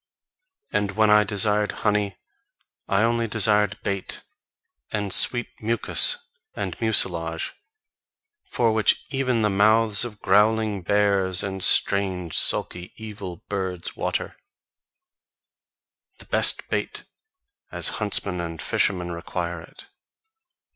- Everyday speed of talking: No, slow, 105 wpm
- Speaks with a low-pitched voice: Yes, low, 100 Hz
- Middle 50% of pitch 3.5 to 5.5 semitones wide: No, average, 2.7 semitones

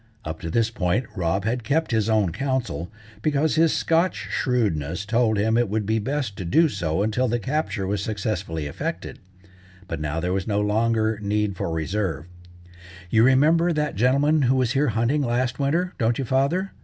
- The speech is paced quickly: No, average, 180 wpm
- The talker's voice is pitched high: No, low, 110 Hz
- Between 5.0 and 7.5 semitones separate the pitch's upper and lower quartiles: Yes, wide, 5.4 semitones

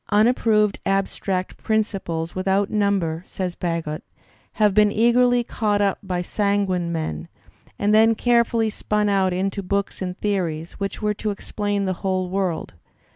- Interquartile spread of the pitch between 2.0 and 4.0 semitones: Yes, narrow, 2.5 semitones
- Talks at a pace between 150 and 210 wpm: No, average, 140 wpm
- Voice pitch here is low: No, high, 200 Hz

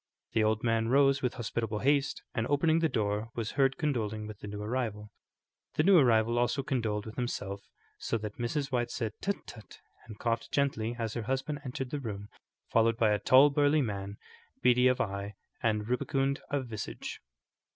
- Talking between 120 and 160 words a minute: No, average, 185 wpm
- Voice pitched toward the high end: No, low, 120 Hz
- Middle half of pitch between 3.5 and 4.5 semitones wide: Yes, average, 3.9 semitones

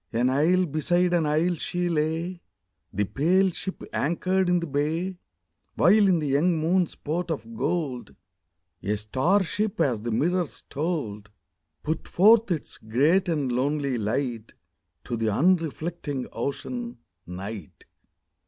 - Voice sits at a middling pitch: Yes, medium, 160 Hz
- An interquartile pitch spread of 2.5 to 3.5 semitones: No, wide, 5.5 semitones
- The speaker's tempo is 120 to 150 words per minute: Yes, slow, 135 wpm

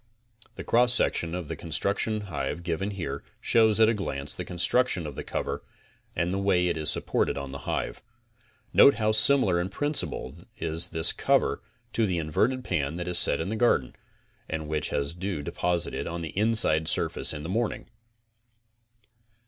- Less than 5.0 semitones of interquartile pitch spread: No, average, 5.3 semitones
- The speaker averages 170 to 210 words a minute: Yes, average, 175 wpm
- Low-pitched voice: Yes, very low, 90 Hz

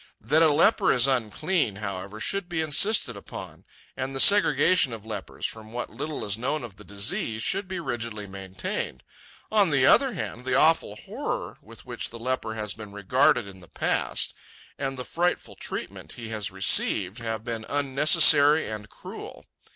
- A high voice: No, low, 120 Hz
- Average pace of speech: Yes, average, 170 wpm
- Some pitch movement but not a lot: No, wide, 6.3 semitones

